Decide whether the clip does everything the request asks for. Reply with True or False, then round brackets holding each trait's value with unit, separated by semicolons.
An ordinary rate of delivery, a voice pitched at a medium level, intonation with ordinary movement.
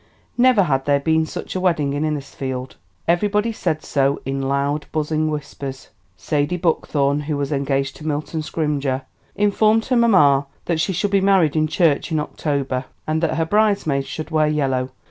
True (170 wpm; 155 Hz; 3.6 semitones)